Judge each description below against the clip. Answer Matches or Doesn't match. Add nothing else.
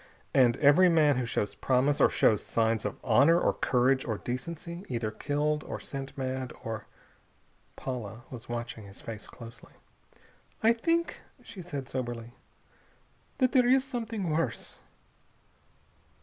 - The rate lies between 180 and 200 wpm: Doesn't match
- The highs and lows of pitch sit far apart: Matches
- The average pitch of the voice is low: Matches